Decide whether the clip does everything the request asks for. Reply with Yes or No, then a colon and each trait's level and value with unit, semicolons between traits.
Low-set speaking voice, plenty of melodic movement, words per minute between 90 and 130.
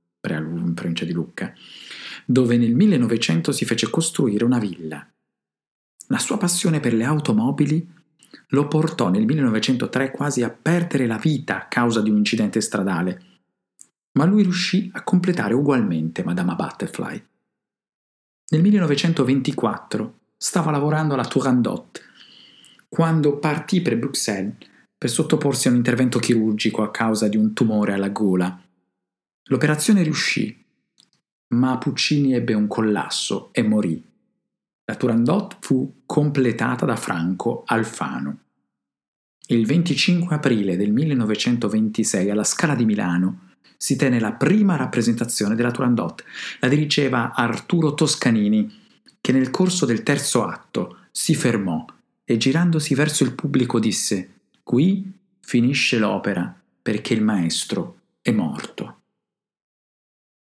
Yes: low, 125 Hz; wide, 6.1 semitones; average, 120 wpm